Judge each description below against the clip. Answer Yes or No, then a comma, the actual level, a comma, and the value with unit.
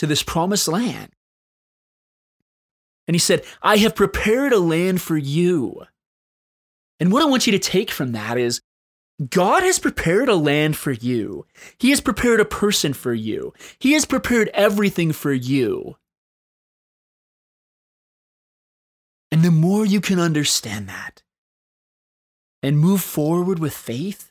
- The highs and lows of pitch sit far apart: Yes, wide, 6.2 semitones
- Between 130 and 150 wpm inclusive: Yes, average, 140 wpm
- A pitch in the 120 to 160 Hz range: No, medium, 175 Hz